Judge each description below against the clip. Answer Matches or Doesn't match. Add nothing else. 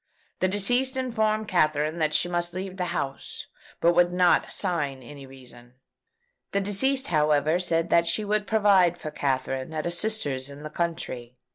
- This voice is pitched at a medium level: Matches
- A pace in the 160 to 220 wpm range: Matches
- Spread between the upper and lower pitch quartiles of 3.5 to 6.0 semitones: Matches